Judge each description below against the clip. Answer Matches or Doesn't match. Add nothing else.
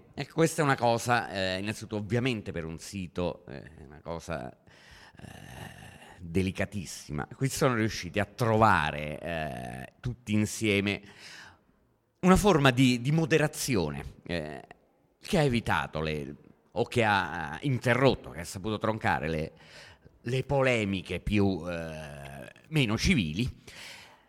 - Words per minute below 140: Matches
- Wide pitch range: Matches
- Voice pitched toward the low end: Matches